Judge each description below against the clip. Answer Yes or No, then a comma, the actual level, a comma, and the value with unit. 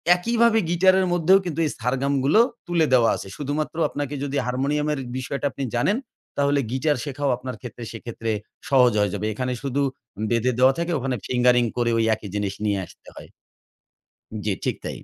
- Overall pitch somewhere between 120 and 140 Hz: Yes, low, 135 Hz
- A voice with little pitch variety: No, average, 3.7 semitones